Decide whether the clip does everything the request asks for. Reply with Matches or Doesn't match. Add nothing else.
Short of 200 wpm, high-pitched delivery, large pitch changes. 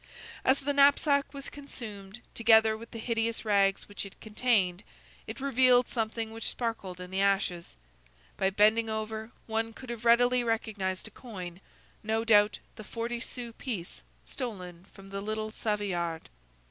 Doesn't match